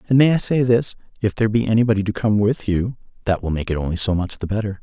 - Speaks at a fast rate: Yes, fast, 275 wpm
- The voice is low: Yes, low, 105 Hz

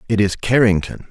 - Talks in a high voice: No, low, 105 Hz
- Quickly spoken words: No, average, 160 wpm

